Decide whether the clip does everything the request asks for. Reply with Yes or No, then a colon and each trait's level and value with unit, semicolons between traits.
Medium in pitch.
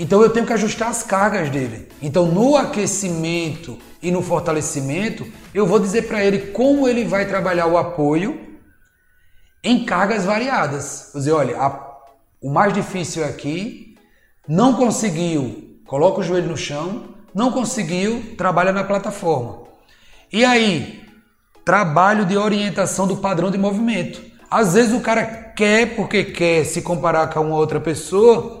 No: high, 195 Hz